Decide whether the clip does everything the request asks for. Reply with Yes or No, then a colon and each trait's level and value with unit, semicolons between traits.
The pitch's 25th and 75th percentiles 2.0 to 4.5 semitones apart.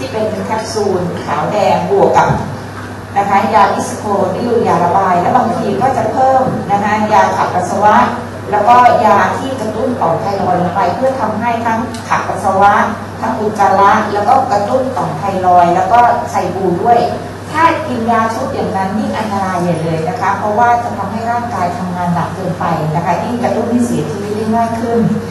Yes: average, 3.9 semitones